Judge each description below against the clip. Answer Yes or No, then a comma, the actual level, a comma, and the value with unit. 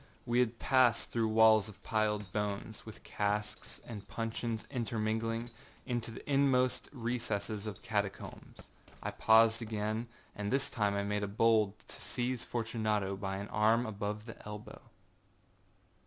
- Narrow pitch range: Yes, narrow, 2.0 semitones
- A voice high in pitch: No, low, 110 Hz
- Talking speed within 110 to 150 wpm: Yes, average, 140 wpm